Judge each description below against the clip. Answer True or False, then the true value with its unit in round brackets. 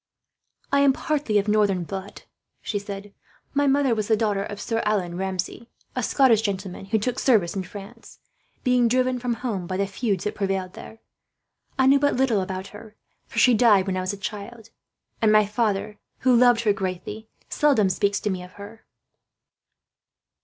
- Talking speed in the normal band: True (180 wpm)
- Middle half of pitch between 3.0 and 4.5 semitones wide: True (3.5 semitones)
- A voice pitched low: False (210 Hz)